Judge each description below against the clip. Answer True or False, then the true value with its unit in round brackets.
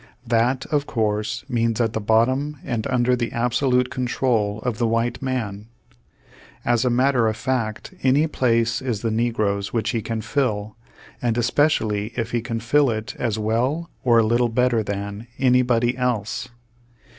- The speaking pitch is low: True (120 Hz)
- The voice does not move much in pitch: True (2.3 semitones)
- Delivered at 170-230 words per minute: False (160 wpm)